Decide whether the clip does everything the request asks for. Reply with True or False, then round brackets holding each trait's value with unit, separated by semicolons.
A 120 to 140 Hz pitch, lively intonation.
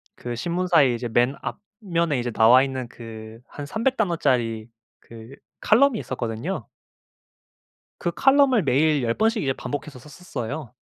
True (135 Hz; 7.0 semitones)